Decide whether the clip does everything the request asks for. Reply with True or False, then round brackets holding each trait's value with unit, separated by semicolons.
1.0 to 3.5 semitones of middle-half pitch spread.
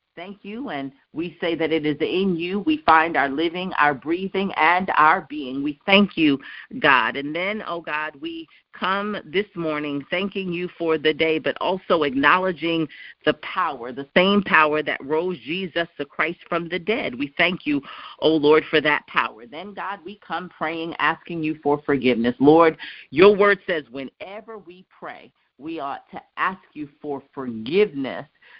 False (4.2 semitones)